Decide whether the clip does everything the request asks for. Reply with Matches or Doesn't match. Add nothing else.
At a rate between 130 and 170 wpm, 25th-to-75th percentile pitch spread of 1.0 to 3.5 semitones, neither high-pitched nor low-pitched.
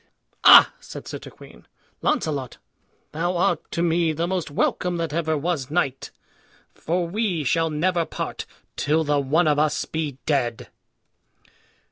Matches